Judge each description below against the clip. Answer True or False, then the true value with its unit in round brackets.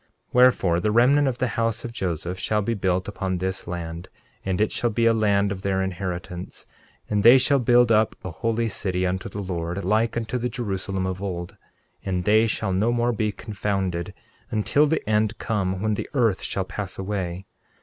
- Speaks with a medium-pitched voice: False (100 Hz)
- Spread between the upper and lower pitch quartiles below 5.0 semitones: True (3.6 semitones)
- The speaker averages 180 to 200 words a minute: True (195 wpm)